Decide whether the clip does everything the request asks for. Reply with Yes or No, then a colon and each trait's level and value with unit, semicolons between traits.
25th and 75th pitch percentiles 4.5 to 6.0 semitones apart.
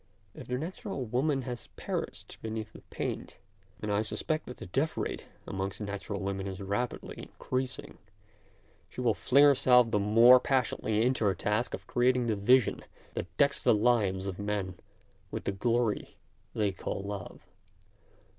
No: average, 3.9 semitones